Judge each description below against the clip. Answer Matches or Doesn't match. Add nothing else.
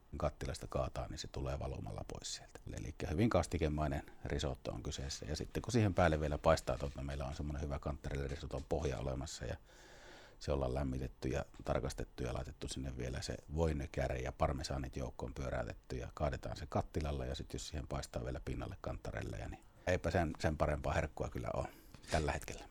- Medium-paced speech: Doesn't match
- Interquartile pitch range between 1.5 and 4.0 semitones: Matches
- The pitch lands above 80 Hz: Doesn't match